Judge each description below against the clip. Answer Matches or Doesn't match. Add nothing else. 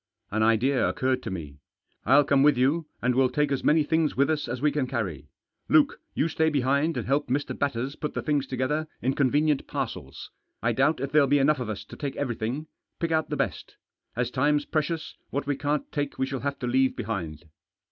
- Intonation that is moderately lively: Matches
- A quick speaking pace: Matches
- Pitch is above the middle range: Doesn't match